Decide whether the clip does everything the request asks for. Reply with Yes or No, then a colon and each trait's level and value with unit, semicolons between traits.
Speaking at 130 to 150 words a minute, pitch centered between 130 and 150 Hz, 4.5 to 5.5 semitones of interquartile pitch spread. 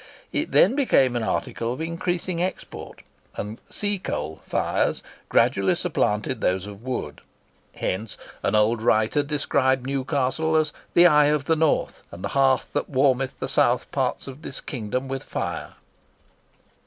Yes: average, 145 wpm; low, 135 Hz; average, 5.2 semitones